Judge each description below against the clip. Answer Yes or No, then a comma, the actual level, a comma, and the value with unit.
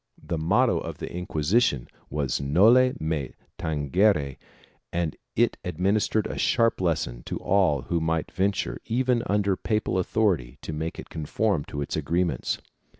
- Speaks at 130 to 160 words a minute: Yes, average, 150 wpm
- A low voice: Yes, very low, 85 Hz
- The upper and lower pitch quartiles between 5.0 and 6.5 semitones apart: Yes, wide, 5.6 semitones